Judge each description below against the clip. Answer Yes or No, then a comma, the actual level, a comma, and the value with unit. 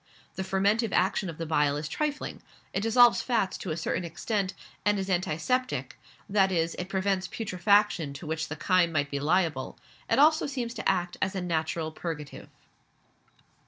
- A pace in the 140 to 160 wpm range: No, average, 170 wpm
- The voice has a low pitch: No, medium, 185 Hz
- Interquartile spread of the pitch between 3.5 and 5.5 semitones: Yes, average, 4.4 semitones